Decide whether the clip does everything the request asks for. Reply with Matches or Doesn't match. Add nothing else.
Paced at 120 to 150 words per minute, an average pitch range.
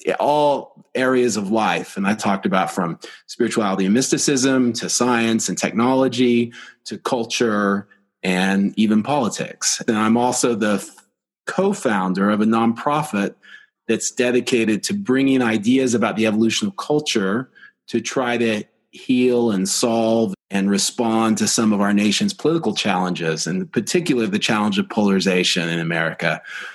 Matches